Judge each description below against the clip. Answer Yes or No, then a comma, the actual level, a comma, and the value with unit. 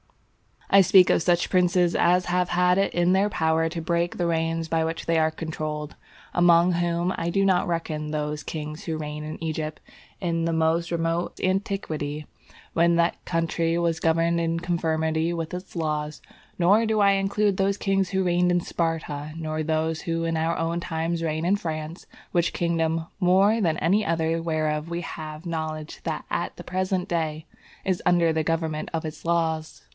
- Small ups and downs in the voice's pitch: Yes, narrow, 1.8 semitones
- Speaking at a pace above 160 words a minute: Yes, average, 180 wpm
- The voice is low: No, medium, 165 Hz